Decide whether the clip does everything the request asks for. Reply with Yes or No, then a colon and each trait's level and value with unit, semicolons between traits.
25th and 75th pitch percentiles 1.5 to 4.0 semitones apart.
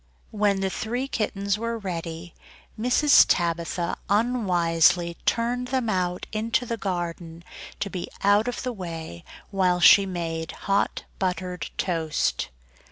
No: average, 4.4 semitones